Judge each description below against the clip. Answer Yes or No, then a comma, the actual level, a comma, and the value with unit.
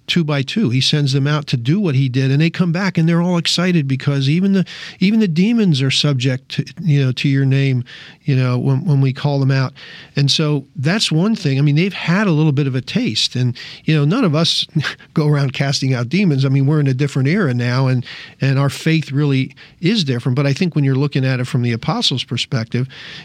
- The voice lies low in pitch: No, medium, 145 Hz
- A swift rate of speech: Yes, fast, 245 wpm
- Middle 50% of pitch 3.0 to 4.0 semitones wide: Yes, average, 3.4 semitones